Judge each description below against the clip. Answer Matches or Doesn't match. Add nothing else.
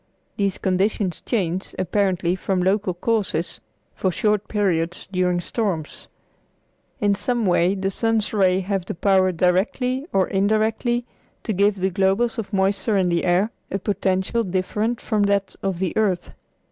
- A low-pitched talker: Doesn't match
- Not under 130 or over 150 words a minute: Matches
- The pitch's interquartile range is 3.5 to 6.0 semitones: Doesn't match